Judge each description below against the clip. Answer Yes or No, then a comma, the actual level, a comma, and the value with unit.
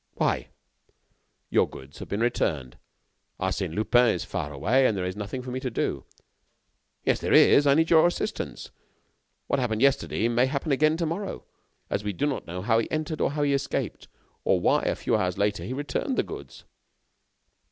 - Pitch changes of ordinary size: No, wide, 6.3 semitones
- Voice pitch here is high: No, low, 125 Hz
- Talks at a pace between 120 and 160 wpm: No, average, 185 wpm